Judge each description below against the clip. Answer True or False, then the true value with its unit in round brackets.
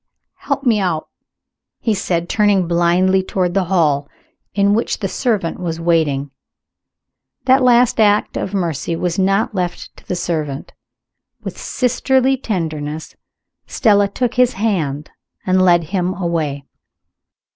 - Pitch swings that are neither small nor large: True (4.0 semitones)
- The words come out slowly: True (130 wpm)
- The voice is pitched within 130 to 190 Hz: True (185 Hz)